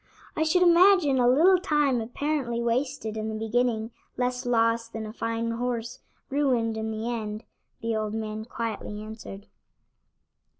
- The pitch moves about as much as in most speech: Yes, average, 3.2 semitones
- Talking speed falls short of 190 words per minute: Yes, average, 145 wpm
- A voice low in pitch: No, high, 235 Hz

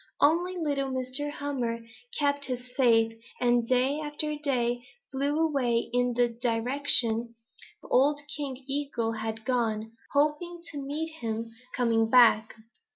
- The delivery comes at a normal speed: No, slow, 125 wpm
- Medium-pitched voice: No, very high, 255 Hz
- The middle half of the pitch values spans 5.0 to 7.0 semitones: No, average, 3.7 semitones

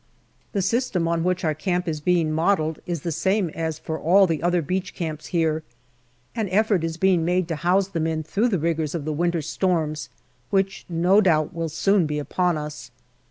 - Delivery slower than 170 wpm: No, average, 200 wpm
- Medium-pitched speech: Yes, medium, 170 Hz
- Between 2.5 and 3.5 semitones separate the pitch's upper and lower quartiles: Yes, average, 2.8 semitones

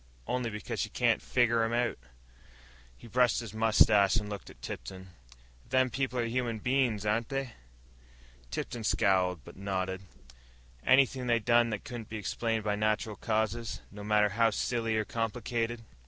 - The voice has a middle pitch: No, low, 115 Hz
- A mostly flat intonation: Yes, narrow, 2.3 semitones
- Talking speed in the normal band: Yes, average, 155 wpm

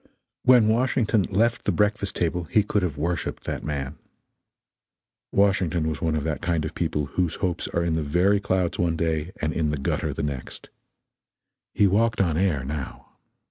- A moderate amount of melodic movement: Yes, average, 4.3 semitones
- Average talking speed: Yes, average, 180 wpm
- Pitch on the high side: No, very low, 85 Hz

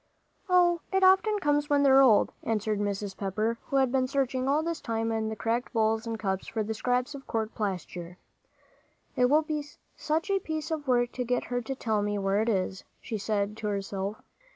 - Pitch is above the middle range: Yes, high, 230 Hz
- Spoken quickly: Yes, fast, 215 wpm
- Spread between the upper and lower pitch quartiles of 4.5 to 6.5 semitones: Yes, average, 5.1 semitones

